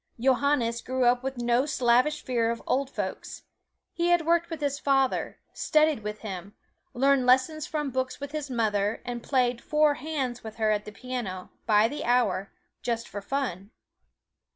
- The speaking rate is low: No, average, 170 wpm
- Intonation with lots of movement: No, average, 3.8 semitones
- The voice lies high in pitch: Yes, very high, 250 Hz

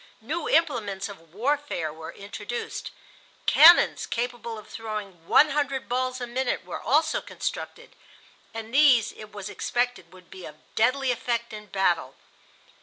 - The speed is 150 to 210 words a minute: No, average, 140 wpm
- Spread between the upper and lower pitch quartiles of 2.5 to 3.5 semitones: No, average, 4.8 semitones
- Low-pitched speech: No, high, 230 Hz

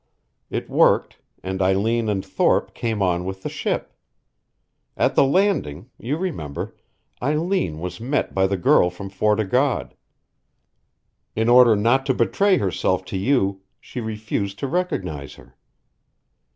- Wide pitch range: Yes, wide, 5.7 semitones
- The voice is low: Yes, low, 105 Hz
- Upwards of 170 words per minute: No, average, 140 wpm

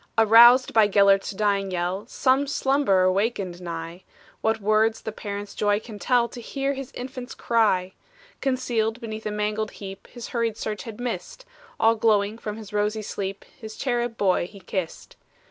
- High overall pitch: Yes, high, 215 Hz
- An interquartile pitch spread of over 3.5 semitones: No, average, 2.9 semitones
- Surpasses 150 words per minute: Yes, average, 165 wpm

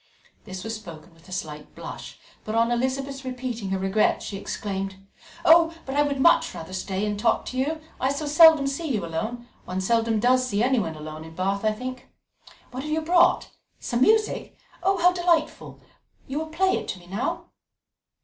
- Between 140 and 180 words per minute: No, average, 190 wpm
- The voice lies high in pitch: Yes, high, 240 Hz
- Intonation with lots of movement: Yes, wide, 7.1 semitones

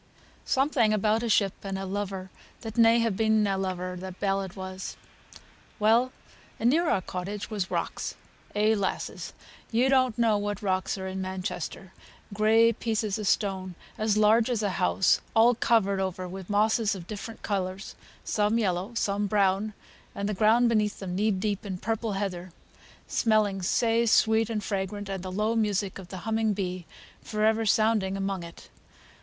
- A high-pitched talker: Yes, high, 205 Hz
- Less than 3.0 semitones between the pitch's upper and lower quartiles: Yes, narrow, 2.6 semitones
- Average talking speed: Yes, average, 170 wpm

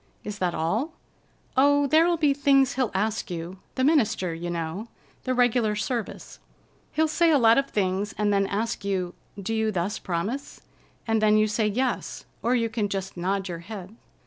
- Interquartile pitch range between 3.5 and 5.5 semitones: Yes, average, 5.0 semitones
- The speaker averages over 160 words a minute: Yes, average, 175 wpm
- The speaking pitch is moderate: No, high, 215 Hz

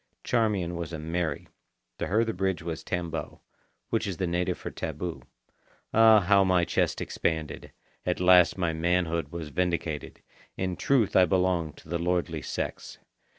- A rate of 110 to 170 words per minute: Yes, average, 155 wpm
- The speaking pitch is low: Yes, very low, 90 Hz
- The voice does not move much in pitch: Yes, narrow, 2.0 semitones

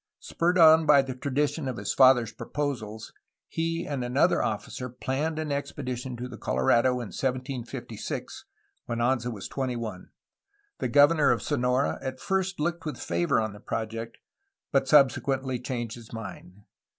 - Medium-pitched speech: No, low, 130 Hz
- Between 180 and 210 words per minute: No, average, 155 wpm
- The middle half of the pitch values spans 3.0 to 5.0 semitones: Yes, average, 3.5 semitones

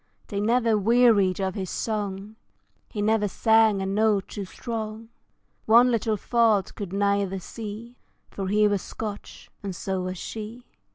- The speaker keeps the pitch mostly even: Yes, narrow, 2.3 semitones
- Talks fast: No, average, 150 wpm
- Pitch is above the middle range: Yes, high, 210 Hz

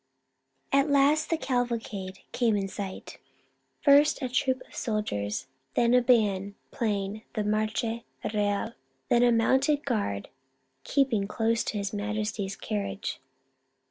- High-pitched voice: Yes, high, 220 Hz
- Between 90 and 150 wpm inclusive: Yes, slow, 135 wpm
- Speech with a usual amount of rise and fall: Yes, average, 3.6 semitones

